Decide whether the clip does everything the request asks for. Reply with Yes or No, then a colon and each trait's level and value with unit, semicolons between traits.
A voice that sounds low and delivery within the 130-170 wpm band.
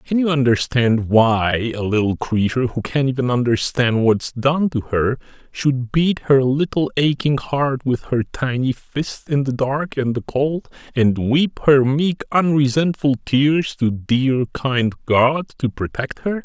Yes: low, 130 Hz; average, 160 wpm